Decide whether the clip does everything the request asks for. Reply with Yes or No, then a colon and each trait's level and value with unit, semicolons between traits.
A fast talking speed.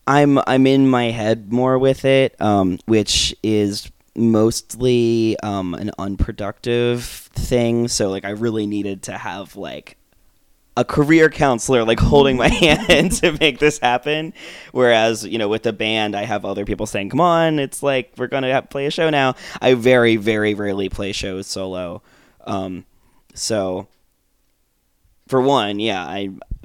No: average, 160 wpm